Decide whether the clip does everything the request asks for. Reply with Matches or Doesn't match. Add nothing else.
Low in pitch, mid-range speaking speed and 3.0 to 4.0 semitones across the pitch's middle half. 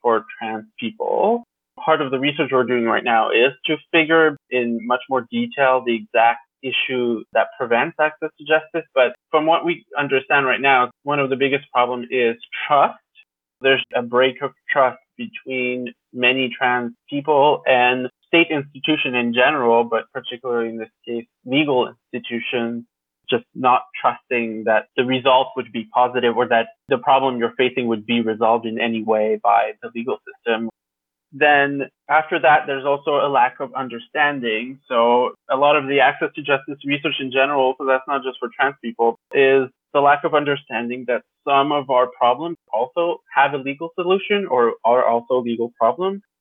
Matches